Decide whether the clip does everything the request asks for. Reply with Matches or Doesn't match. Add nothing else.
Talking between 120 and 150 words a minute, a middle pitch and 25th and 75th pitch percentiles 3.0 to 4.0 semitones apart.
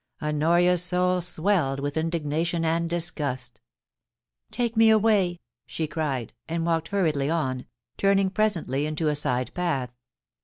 Matches